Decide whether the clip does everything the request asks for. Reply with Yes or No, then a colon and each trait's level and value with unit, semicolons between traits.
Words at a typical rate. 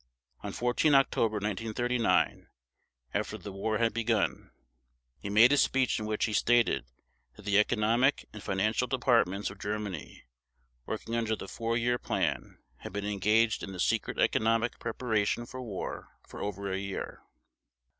Yes: average, 150 wpm